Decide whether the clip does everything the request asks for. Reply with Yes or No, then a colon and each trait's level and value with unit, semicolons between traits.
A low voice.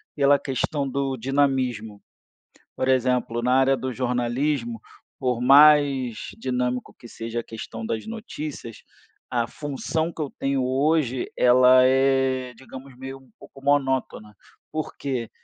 Yes: low, 130 Hz